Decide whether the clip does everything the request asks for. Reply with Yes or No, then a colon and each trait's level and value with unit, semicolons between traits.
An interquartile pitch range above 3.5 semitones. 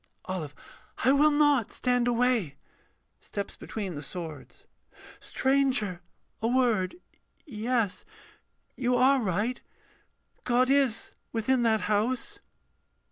Yes: average, 4.2 semitones